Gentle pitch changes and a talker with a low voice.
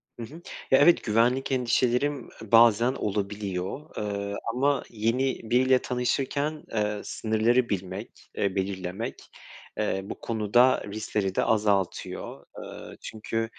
No: average, 3.7 semitones; low, 115 Hz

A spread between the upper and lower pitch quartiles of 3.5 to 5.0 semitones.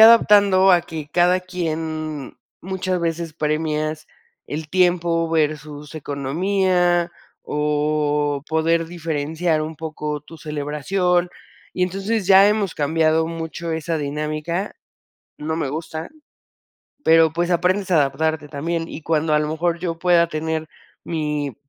No: narrow, 2.5 semitones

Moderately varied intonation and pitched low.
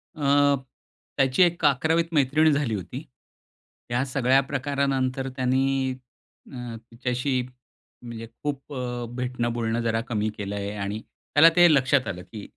Yes: average, 3.2 semitones; low, 130 Hz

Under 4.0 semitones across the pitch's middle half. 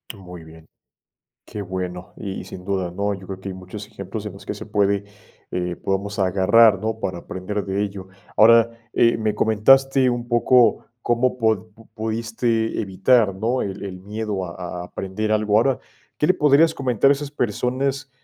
Yes: average, 3.5 semitones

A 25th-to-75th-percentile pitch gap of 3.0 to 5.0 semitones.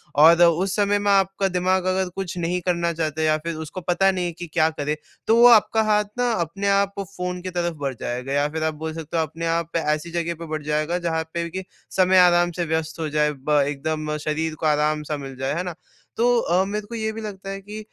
Yes: average, 3.4 semitones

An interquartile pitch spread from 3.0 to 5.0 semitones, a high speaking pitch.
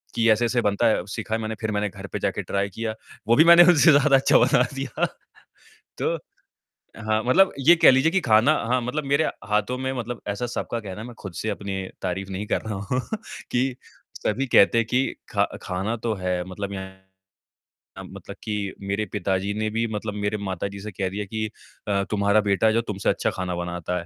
No: average, 3.7 semitones; low, 110 Hz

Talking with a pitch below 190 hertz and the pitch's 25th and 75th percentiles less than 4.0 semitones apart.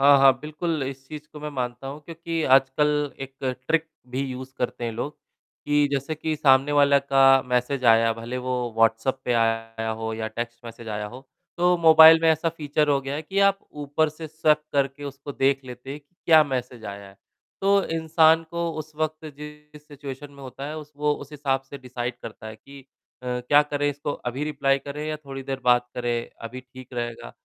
Yes: medium, 140 Hz; average, 3.3 semitones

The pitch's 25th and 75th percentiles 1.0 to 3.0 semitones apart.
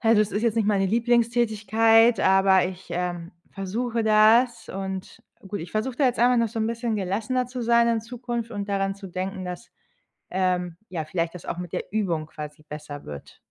No: average, 4.1 semitones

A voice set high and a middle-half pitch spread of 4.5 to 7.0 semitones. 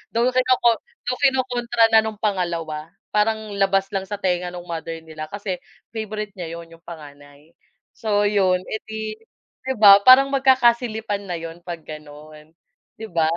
Yes: high, 200 Hz; average, 5.0 semitones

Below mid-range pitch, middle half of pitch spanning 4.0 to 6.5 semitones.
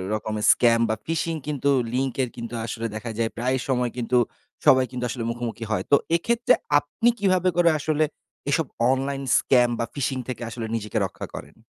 Yes: low, 130 Hz; average, 4.3 semitones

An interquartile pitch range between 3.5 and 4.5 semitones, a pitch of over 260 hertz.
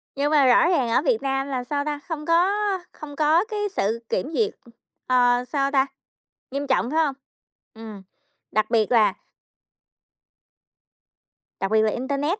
Yes: average, 3.8 semitones; very high, 275 Hz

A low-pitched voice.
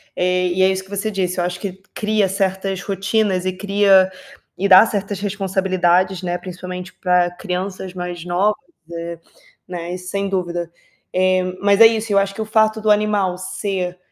No: high, 190 Hz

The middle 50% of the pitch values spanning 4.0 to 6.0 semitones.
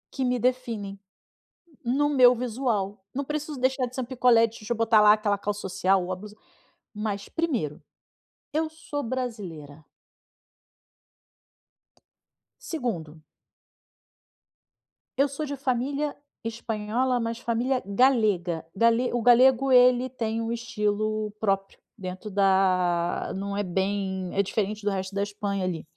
Yes: average, 4.3 semitones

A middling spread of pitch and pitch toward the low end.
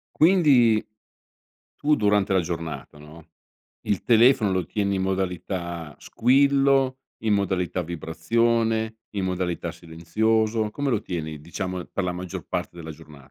Yes: average, 4.7 semitones; very low, 95 Hz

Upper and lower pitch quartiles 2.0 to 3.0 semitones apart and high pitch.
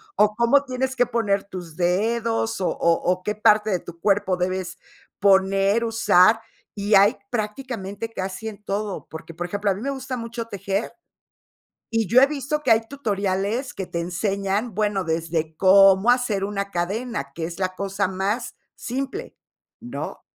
No: average, 3.4 semitones; high, 205 Hz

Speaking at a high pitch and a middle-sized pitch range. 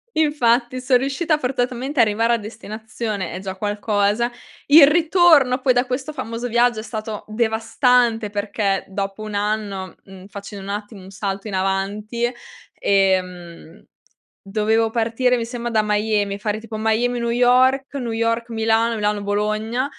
Yes: high, 225 Hz; average, 3.1 semitones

